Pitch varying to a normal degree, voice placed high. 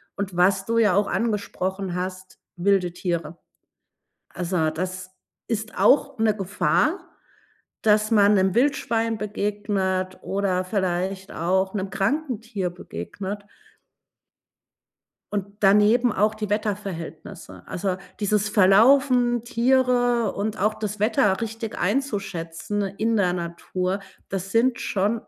Yes: average, 3.1 semitones; high, 200 Hz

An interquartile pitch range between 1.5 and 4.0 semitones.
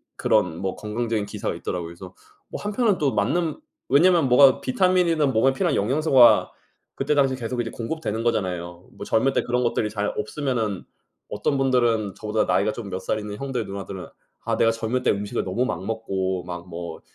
No: average, 5.3 semitones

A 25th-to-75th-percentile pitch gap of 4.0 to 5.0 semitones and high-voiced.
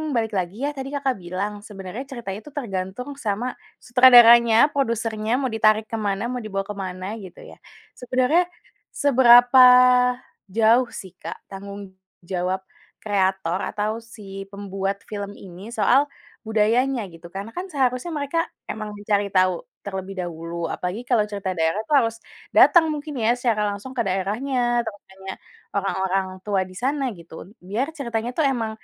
Yes: average, 4.3 semitones; high, 215 Hz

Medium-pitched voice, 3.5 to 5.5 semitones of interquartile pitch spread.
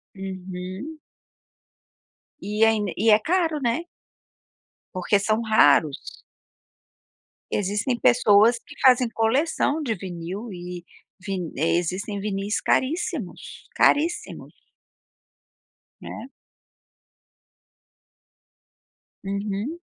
No: high, 210 Hz; average, 4.5 semitones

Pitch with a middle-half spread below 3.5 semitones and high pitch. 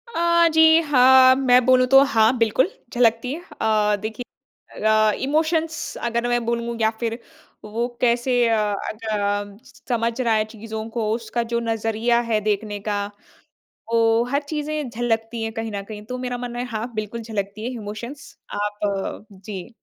Yes: narrow, 2.6 semitones; high, 230 Hz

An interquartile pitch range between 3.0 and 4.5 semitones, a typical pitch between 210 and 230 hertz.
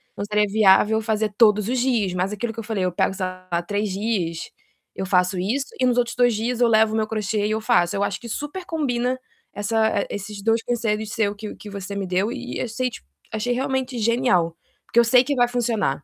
Yes: average, 3.3 semitones; high, 220 Hz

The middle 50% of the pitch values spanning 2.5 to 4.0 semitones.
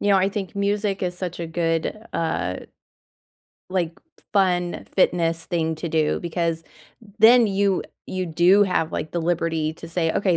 Yes: average, 2.9 semitones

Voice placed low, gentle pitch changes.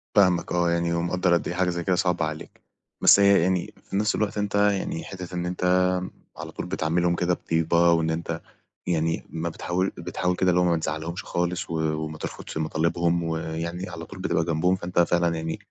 Yes: very low, 85 Hz; narrow, 1.6 semitones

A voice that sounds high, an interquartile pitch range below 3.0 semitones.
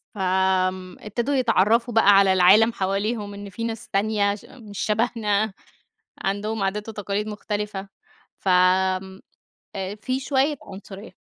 Yes: high, 205 Hz; narrow, 2.6 semitones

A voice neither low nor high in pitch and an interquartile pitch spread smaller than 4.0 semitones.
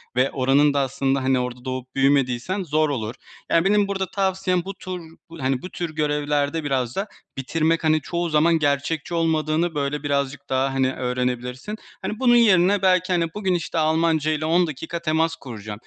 No: medium, 155 Hz; average, 4.4 semitones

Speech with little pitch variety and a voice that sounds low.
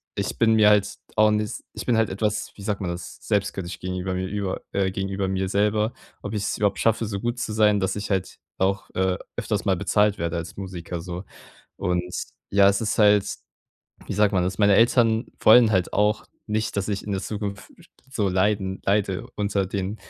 Yes: narrow, 2.0 semitones; low, 100 Hz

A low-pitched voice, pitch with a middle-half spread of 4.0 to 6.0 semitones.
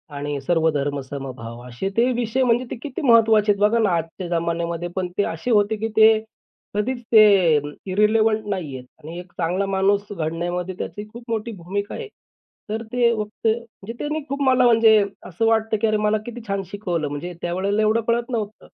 No: high, 205 Hz; average, 4.7 semitones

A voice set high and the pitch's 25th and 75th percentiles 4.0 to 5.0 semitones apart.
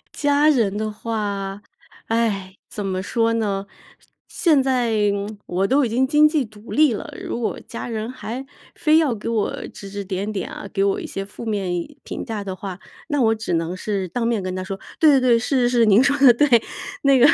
Yes: high, 220 Hz; average, 4.3 semitones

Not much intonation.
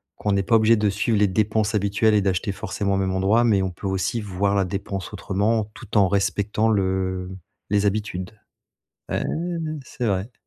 Yes: narrow, 1.9 semitones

